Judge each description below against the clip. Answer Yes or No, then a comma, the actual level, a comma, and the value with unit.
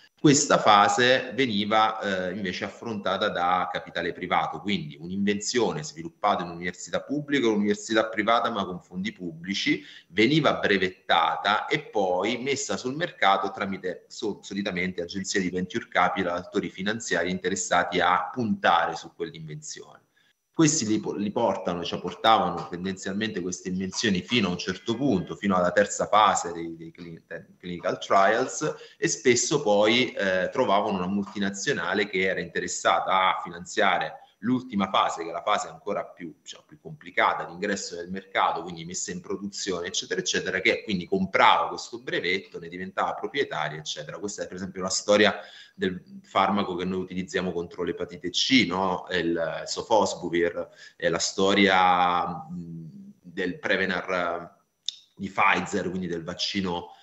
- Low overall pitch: Yes, very low, 95 Hz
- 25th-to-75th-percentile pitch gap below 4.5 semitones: Yes, average, 3.7 semitones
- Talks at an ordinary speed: Yes, average, 140 wpm